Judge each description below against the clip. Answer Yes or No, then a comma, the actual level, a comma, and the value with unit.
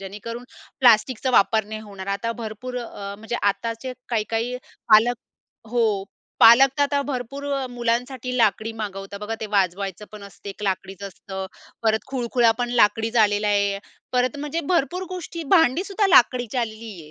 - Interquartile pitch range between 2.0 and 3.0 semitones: No, average, 3.5 semitones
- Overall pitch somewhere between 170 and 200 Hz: No, high, 225 Hz